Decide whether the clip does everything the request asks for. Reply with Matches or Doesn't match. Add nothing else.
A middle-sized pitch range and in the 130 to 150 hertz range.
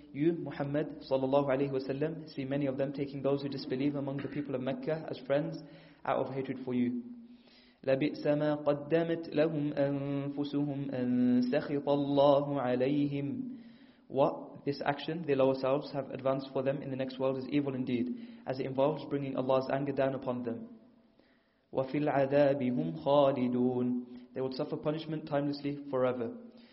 Doesn't match